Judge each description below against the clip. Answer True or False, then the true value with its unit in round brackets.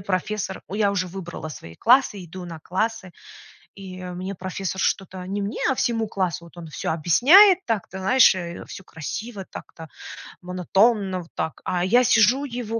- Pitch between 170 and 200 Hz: True (190 Hz)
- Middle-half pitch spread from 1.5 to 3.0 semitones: False (3.7 semitones)